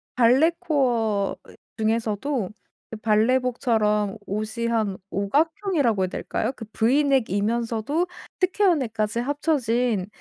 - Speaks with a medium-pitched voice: No, high, 230 Hz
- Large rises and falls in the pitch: No, average, 4.4 semitones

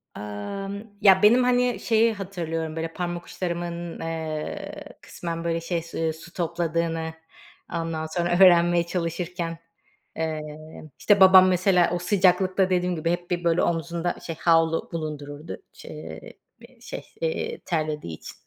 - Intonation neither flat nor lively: No, narrow, 2.1 semitones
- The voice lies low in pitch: No, medium, 170 Hz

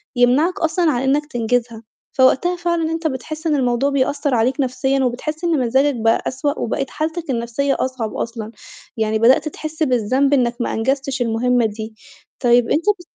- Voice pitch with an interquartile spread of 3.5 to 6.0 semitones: Yes, average, 3.8 semitones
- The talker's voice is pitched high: Yes, very high, 260 Hz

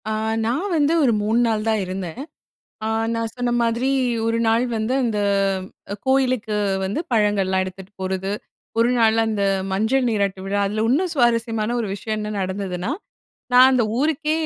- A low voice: No, high, 225 Hz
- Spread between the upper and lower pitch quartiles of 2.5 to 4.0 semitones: Yes, average, 3.5 semitones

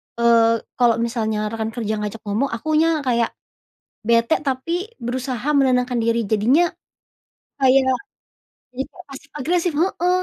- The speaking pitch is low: No, very high, 250 Hz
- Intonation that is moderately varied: Yes, average, 3.0 semitones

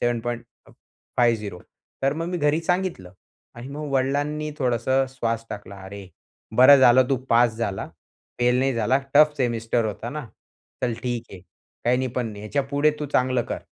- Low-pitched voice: Yes, low, 125 Hz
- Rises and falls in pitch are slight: No, average, 3.6 semitones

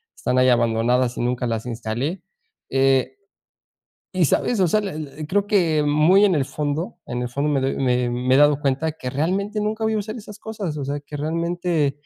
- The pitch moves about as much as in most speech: No, wide, 6.1 semitones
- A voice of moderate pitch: Yes, medium, 150 Hz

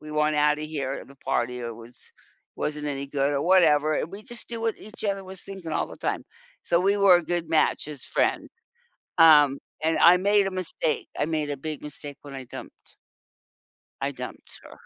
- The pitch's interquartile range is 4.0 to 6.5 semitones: Yes, average, 4.3 semitones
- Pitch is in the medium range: Yes, medium, 155 Hz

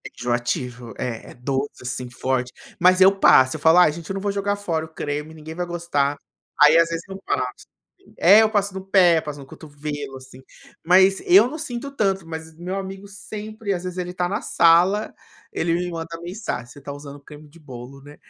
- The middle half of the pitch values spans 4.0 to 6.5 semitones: Yes, average, 5.1 semitones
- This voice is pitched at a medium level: Yes, medium, 165 Hz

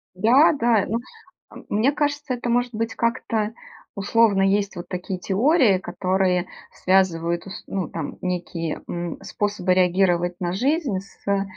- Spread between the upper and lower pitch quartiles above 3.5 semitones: Yes, average, 4.2 semitones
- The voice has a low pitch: No, high, 195 Hz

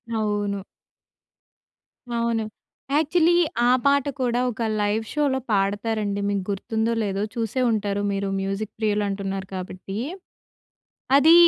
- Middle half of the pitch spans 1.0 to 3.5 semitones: Yes, average, 2.9 semitones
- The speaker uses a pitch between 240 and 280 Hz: No, high, 210 Hz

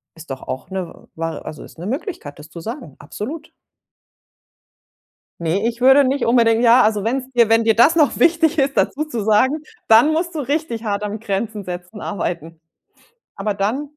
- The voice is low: No, high, 225 Hz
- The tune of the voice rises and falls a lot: Yes, wide, 5.7 semitones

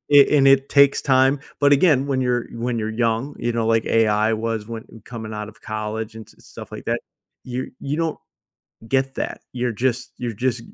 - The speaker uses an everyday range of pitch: Yes, average, 3.3 semitones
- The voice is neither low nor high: No, low, 120 Hz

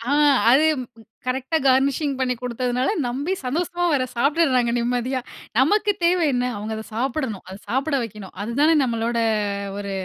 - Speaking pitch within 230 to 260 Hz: Yes, very high, 255 Hz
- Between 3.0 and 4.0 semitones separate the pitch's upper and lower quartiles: Yes, average, 3.3 semitones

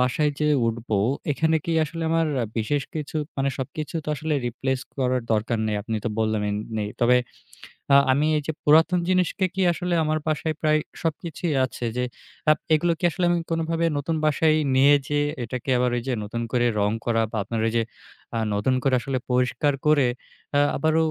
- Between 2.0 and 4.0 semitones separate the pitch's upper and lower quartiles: No, average, 4.6 semitones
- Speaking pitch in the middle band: Yes, medium, 145 Hz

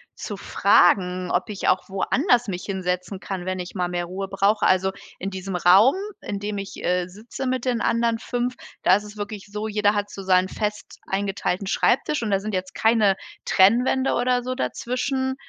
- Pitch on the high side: Yes, high, 200 Hz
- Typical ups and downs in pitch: Yes, average, 3.6 semitones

